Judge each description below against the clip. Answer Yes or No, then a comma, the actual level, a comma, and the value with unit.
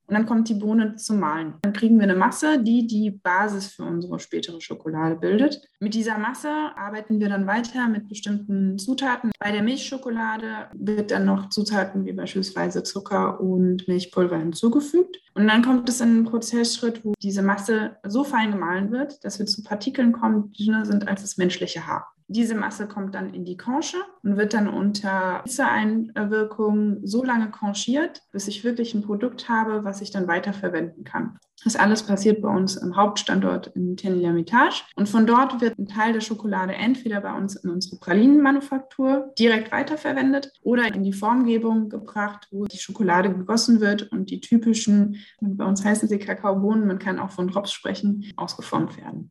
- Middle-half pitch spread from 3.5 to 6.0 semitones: No, average, 2.9 semitones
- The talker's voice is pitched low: No, high, 210 Hz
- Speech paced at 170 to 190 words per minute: Yes, average, 180 wpm